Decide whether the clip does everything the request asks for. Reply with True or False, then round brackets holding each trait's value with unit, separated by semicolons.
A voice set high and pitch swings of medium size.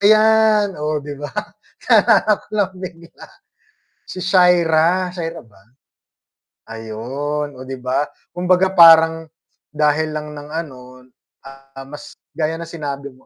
False (160 Hz; 4.3 semitones)